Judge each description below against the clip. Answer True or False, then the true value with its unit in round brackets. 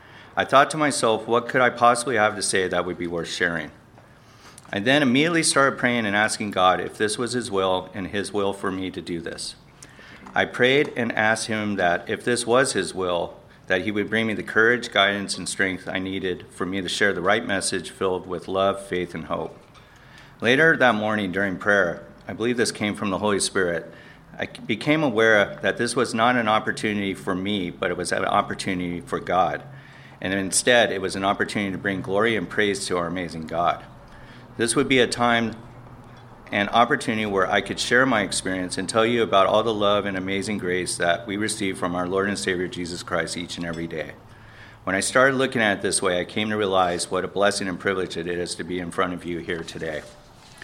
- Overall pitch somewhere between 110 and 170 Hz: False (100 Hz)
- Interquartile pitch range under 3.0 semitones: False (3.5 semitones)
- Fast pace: True (215 wpm)